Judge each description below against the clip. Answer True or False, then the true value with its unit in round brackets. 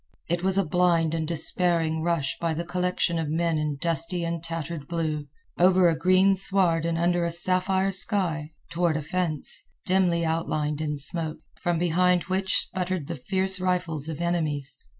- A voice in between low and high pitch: True (170 Hz)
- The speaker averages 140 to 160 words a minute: False (170 wpm)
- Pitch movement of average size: False (2.3 semitones)